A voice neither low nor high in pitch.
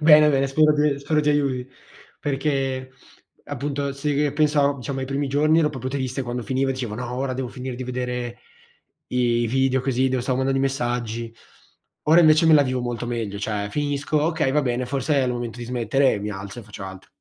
No: low, 130 Hz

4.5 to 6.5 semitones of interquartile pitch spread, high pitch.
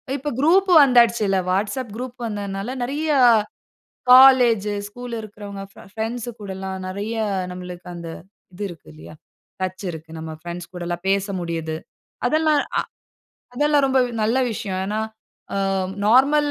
Yes: wide, 5.4 semitones; high, 210 Hz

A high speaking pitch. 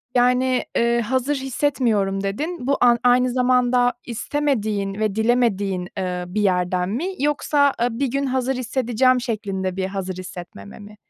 Yes: high, 235 Hz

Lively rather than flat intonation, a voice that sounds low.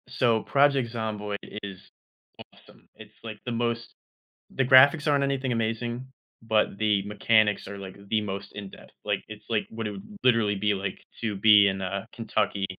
No: average, 2.7 semitones; low, 110 Hz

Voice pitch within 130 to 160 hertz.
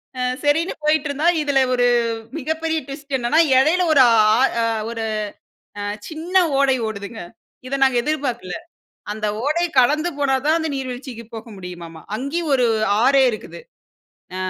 No: very high, 270 Hz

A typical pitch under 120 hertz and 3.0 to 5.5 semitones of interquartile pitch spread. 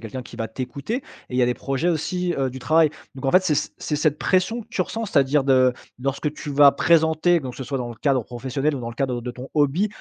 No: medium, 140 Hz; average, 3.9 semitones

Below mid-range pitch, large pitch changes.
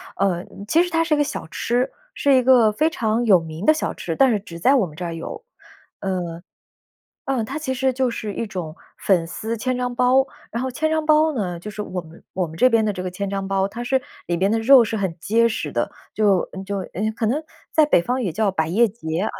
No: high, 220 Hz; wide, 5.8 semitones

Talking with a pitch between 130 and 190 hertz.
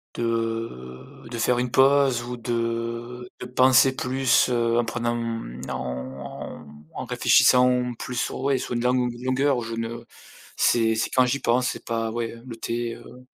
No: low, 120 Hz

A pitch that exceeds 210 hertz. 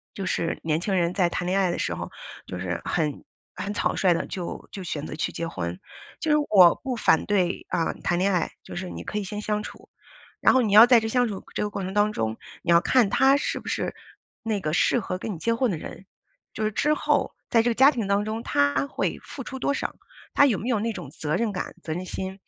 No: high, 195 Hz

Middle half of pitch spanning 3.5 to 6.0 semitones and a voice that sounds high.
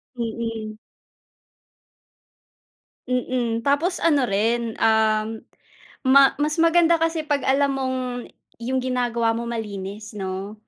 Yes: average, 4.1 semitones; high, 235 Hz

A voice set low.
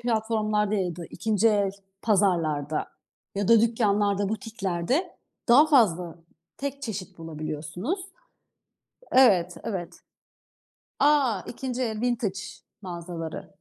No: high, 210 Hz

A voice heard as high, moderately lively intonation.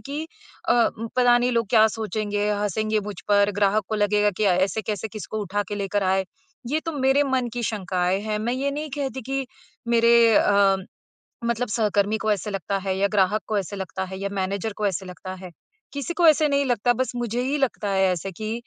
Yes: high, 215 Hz; average, 3.4 semitones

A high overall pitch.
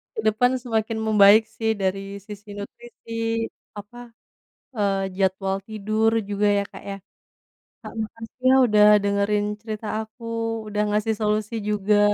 Yes: high, 210 Hz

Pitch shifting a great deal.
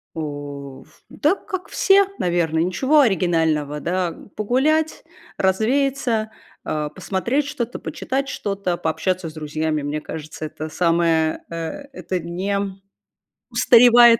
Yes: wide, 7.2 semitones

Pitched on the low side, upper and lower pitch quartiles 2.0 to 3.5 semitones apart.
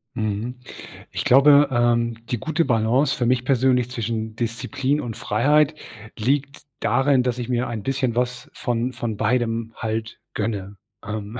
Yes: low, 120 Hz; narrow, 2.6 semitones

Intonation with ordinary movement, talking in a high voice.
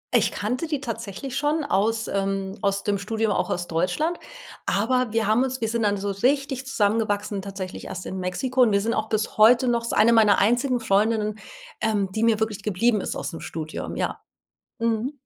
Yes: average, 3.3 semitones; high, 220 Hz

